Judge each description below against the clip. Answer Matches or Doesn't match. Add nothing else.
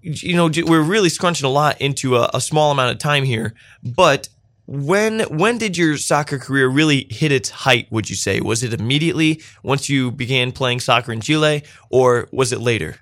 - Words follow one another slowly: Doesn't match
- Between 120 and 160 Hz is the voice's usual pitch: Matches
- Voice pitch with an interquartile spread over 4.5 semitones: Doesn't match